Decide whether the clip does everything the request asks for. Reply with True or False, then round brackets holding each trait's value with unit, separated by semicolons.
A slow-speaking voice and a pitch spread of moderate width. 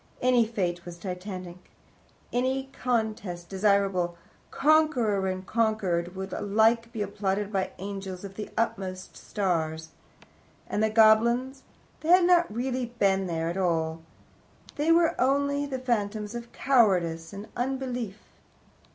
True (130 wpm; 4.8 semitones)